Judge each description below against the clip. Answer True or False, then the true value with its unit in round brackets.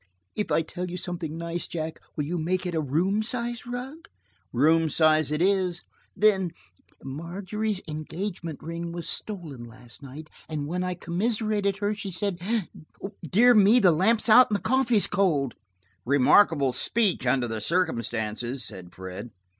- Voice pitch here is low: False (175 Hz)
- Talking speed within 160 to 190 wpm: False (150 wpm)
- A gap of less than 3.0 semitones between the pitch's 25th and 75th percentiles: False (5.2 semitones)